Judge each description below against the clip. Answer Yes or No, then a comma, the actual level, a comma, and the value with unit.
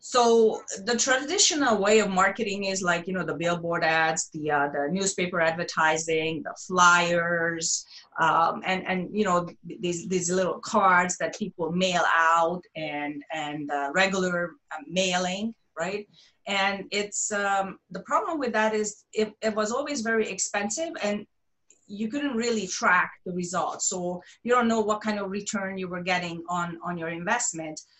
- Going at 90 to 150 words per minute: No, average, 160 wpm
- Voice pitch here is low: No, medium, 185 Hz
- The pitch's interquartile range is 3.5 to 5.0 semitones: Yes, average, 3.8 semitones